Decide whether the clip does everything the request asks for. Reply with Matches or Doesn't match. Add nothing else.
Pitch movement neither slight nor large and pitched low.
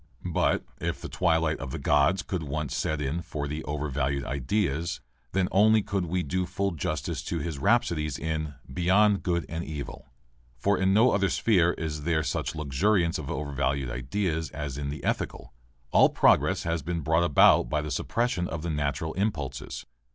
Matches